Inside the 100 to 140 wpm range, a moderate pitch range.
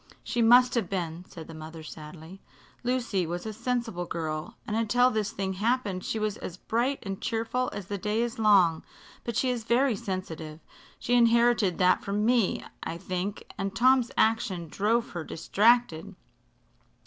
No: average, 165 wpm; average, 4.8 semitones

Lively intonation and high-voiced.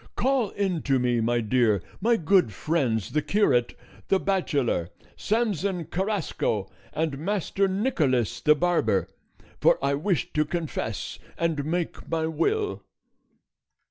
No: wide, 7.6 semitones; medium, 160 Hz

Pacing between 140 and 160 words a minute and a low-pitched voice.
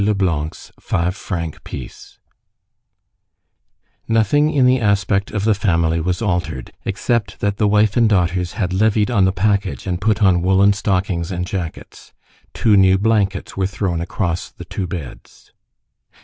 Yes: average, 150 wpm; very low, 95 Hz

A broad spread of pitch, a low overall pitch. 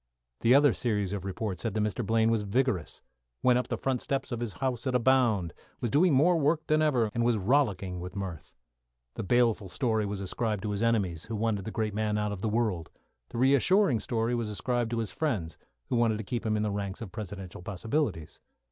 No: average, 3.5 semitones; low, 110 Hz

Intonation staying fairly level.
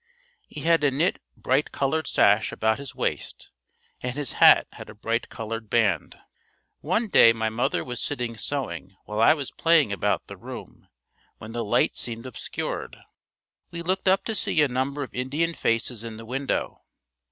No: average, 4.5 semitones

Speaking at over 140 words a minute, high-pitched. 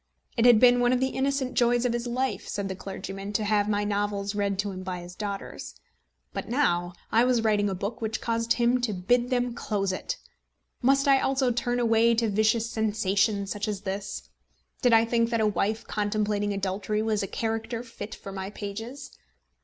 Yes: average, 200 wpm; high, 220 Hz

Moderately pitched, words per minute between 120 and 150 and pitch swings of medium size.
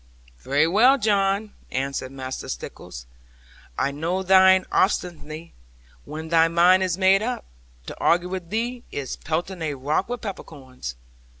Yes: medium, 175 Hz; slow, 135 wpm; average, 4.8 semitones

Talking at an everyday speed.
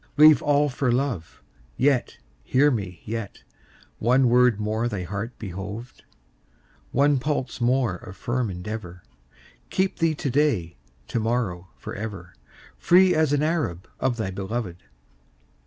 No: slow, 130 wpm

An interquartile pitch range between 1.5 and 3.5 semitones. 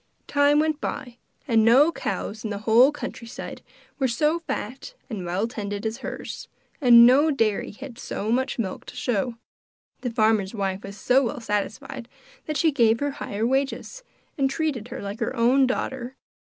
No: average, 4.0 semitones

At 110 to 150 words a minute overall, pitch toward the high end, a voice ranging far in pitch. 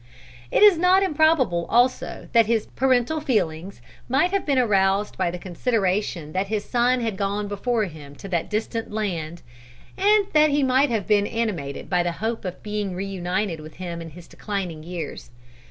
No: average, 175 wpm; high, 205 Hz; wide, 5.8 semitones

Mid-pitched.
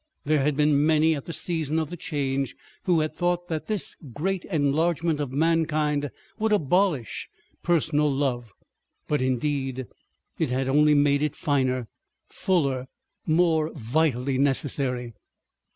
Yes: medium, 150 Hz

